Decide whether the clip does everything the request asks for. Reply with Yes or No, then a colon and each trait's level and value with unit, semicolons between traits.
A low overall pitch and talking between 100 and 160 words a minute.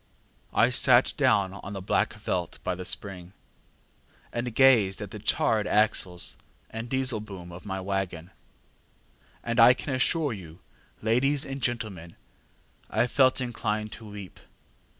Yes: low, 105 Hz; slow, 135 wpm